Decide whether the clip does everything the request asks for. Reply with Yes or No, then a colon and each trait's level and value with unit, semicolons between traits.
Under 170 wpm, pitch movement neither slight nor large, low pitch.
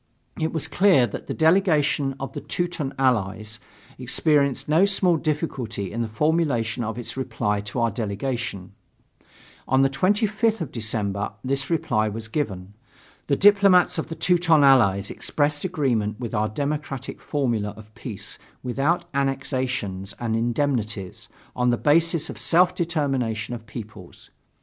No: average, 140 wpm; wide, 6.1 semitones; low, 130 Hz